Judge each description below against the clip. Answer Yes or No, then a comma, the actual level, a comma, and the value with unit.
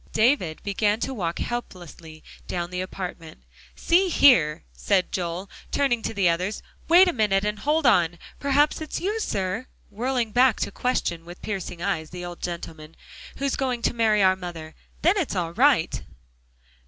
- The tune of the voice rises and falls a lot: Yes, wide, 6.8 semitones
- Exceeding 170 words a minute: No, average, 165 wpm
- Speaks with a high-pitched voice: Yes, high, 200 Hz